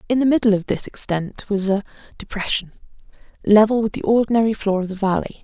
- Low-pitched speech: No, high, 210 Hz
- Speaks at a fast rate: No, average, 190 wpm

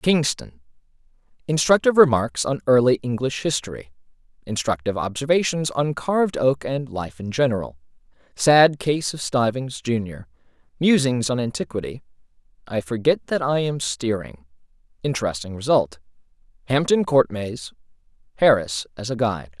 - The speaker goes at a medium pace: No, slow, 95 wpm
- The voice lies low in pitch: Yes, low, 120 Hz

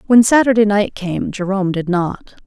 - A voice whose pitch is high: Yes, high, 200 Hz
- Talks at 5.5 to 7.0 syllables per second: No, 5.0 syllables/s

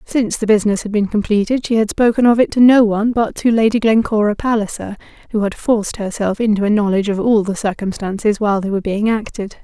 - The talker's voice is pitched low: No, high, 215 Hz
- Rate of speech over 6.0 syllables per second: Yes, 6.4 syllables/s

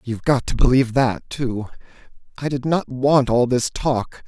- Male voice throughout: Yes, male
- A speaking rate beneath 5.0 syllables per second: Yes, 4.6 syllables/s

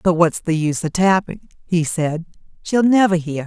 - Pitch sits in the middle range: Yes, medium, 175 Hz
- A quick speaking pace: No, average, 190 wpm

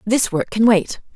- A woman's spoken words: Yes, female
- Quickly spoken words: Yes, fast, 210 wpm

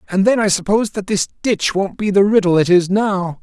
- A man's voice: Yes, male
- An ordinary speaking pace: No, fast, 245 wpm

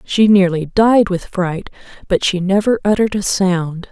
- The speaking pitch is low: No, high, 190 Hz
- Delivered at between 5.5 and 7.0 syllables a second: No, 4.4 syllables/s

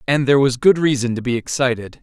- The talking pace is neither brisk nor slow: No, fast, 235 wpm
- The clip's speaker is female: No, male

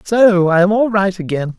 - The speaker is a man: Yes, male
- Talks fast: Yes, fast, 225 wpm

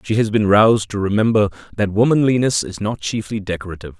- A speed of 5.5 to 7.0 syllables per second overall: Yes, 6.7 syllables/s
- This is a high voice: No, low, 105 Hz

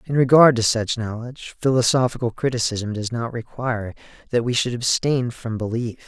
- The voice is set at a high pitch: No, low, 120 Hz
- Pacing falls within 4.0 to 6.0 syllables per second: Yes, 5.3 syllables/s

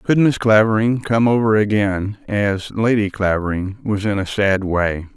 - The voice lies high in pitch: No, low, 105 Hz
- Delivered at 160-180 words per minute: Yes, average, 165 wpm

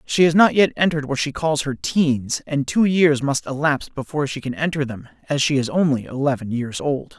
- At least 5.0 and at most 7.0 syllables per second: Yes, 5.4 syllables/s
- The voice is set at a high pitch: No, medium, 145 Hz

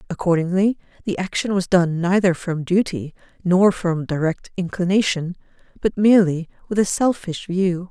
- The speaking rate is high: No, slow, 135 wpm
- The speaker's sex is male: No, female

